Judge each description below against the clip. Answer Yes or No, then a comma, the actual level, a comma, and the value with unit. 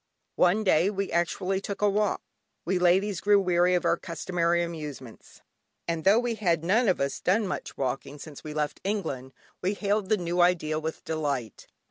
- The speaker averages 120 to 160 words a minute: No, average, 180 wpm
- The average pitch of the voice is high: No, medium, 175 Hz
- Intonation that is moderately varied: Yes, average, 4.0 semitones